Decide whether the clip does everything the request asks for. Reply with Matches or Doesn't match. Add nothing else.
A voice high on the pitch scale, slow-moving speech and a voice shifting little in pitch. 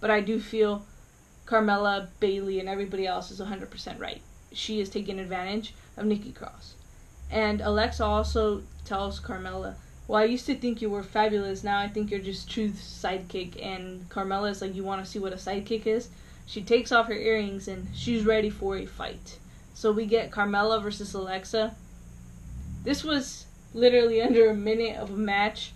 Doesn't match